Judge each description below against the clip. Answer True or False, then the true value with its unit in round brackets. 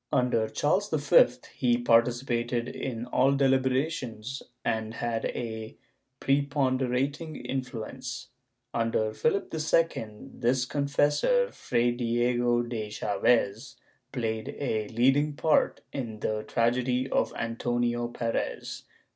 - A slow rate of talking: True (105 wpm)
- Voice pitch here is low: True (120 Hz)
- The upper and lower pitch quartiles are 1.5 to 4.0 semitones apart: True (2.8 semitones)